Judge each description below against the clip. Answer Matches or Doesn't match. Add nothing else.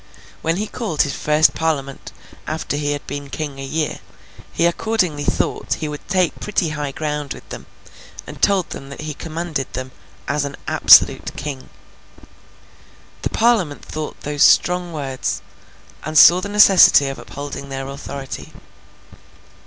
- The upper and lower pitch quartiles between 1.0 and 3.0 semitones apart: Doesn't match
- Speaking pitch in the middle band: Matches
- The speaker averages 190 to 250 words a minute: Doesn't match